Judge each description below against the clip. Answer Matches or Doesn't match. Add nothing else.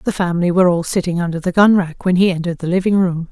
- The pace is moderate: Doesn't match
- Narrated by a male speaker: Doesn't match